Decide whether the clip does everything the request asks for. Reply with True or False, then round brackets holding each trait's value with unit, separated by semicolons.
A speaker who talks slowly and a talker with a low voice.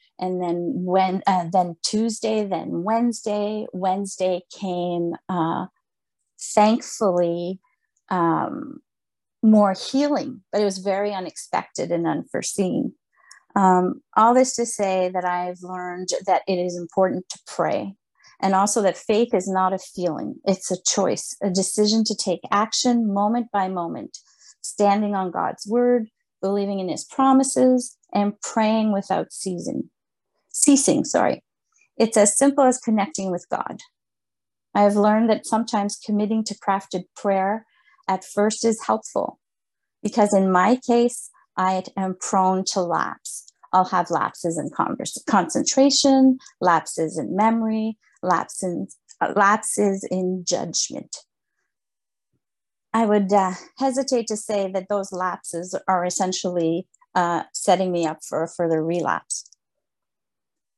False (130 wpm; 200 Hz)